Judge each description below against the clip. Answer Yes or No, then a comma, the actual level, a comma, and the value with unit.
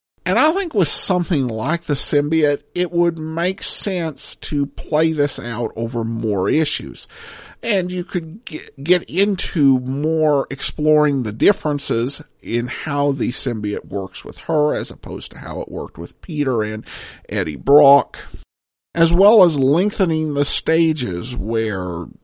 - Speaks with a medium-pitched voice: Yes, medium, 145 Hz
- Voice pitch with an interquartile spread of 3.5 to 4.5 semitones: No, average, 5.3 semitones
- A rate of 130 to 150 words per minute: Yes, average, 145 wpm